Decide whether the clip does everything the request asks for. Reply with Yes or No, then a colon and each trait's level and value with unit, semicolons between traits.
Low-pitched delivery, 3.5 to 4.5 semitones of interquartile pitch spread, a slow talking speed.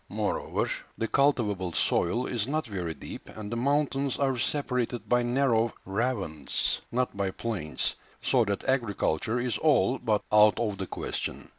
No: low, 115 Hz; average, 4.2 semitones; average, 150 wpm